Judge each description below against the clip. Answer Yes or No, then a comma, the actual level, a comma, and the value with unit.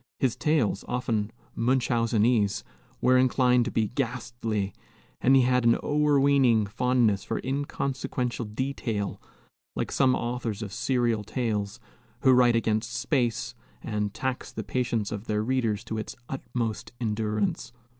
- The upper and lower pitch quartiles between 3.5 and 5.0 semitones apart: No, average, 3.0 semitones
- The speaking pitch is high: No, low, 120 Hz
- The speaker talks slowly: Yes, slow, 130 wpm